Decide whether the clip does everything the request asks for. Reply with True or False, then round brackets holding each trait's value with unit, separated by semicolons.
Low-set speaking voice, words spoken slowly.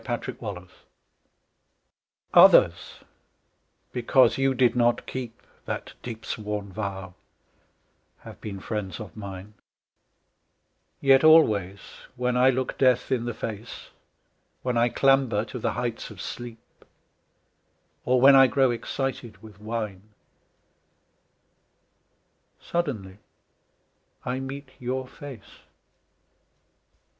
True (120 Hz; 105 wpm)